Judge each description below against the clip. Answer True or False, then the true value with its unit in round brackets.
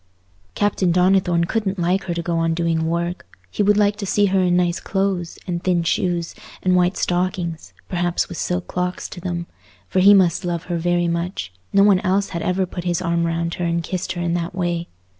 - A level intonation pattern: True (1.6 semitones)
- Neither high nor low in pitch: True (175 Hz)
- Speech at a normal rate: False (210 wpm)